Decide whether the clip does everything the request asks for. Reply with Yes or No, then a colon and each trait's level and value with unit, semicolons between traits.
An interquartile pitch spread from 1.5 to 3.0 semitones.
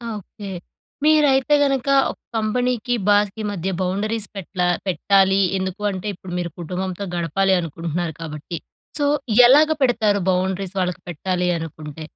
No: average, 3.5 semitones